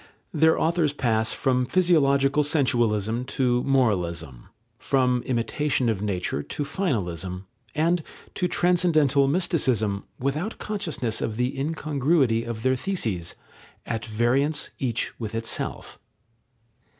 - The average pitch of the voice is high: No, low, 130 Hz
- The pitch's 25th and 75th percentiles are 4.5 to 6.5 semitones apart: Yes, average, 5.2 semitones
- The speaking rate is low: Yes, slow, 110 wpm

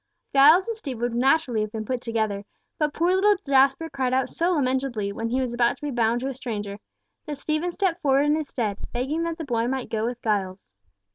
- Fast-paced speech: Yes, fast, 225 wpm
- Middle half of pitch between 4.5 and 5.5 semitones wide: Yes, average, 4.8 semitones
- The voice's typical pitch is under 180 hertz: No, very high, 260 Hz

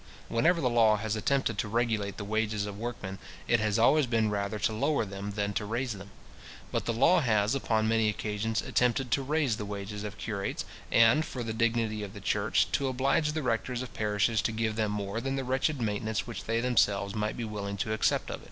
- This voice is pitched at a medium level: No, low, 110 Hz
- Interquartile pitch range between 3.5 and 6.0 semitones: No, average, 2.7 semitones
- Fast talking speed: Yes, fast, 215 wpm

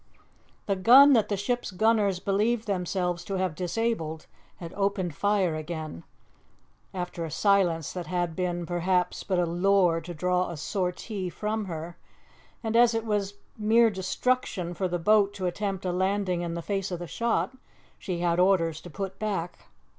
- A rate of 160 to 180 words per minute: Yes, average, 170 wpm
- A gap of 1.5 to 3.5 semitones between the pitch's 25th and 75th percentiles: Yes, average, 2.9 semitones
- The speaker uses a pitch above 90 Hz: Yes, medium, 185 Hz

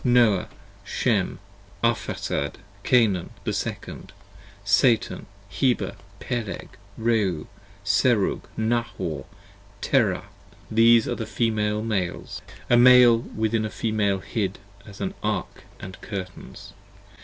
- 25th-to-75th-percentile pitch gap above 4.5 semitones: No, average, 2.9 semitones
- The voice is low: Yes, low, 110 Hz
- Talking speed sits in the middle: No, slow, 110 wpm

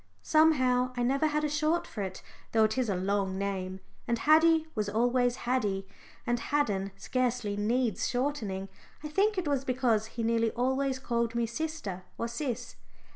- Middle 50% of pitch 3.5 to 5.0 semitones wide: Yes, average, 4.7 semitones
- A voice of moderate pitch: No, high, 245 Hz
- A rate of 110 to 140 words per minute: No, average, 170 wpm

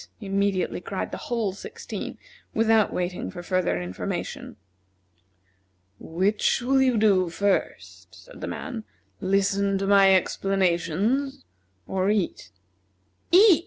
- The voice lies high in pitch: Yes, high, 195 Hz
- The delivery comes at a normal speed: No, slow, 110 wpm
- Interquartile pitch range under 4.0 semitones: Yes, average, 3.2 semitones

